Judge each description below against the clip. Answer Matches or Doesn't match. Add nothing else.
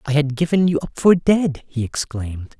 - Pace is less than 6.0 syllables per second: Matches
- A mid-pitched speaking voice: Matches